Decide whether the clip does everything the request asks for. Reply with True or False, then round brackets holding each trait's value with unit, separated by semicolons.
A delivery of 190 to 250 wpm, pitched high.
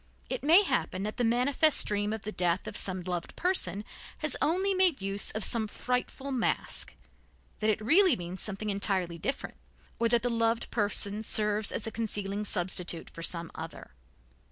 False (175 wpm; 215 Hz)